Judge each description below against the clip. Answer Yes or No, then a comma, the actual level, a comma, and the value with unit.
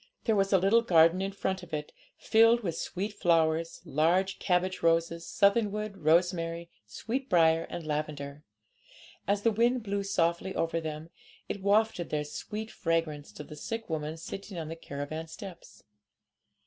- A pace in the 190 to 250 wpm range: No, average, 150 wpm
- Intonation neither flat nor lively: Yes, average, 3.8 semitones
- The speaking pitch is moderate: Yes, medium, 170 Hz